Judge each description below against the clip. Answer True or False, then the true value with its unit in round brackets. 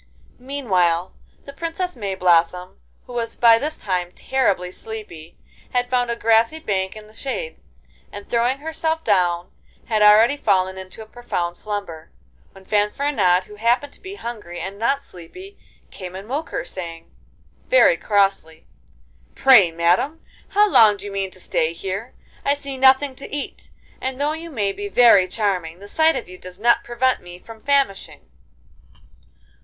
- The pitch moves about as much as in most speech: False (6.4 semitones)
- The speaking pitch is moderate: False (215 Hz)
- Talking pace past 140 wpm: True (160 wpm)